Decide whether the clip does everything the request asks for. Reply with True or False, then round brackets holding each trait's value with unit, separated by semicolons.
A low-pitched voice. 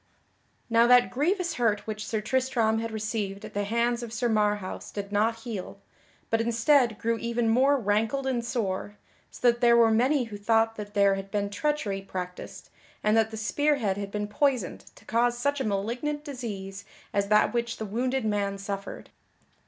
False (225 Hz)